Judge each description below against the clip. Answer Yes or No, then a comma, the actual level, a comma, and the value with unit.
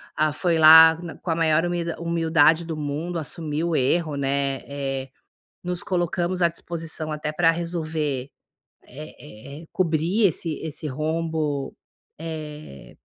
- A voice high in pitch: No, medium, 160 Hz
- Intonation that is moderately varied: No, narrow, 2.1 semitones